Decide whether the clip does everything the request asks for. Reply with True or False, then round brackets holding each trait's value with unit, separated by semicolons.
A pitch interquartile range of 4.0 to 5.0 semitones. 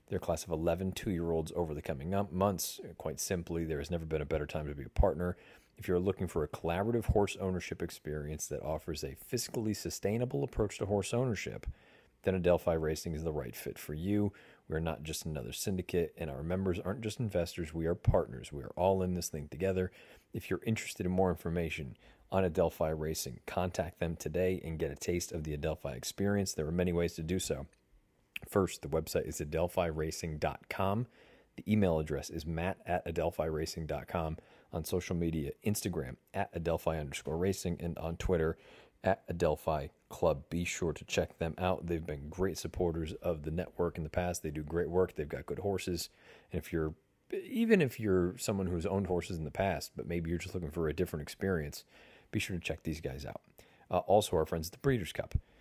False (3.1 semitones)